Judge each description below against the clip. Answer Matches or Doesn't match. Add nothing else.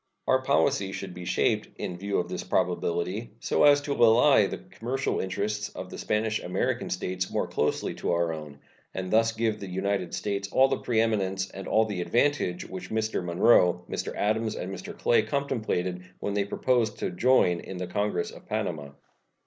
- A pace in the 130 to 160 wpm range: Doesn't match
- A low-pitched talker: Matches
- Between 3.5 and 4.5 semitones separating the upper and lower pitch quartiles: Matches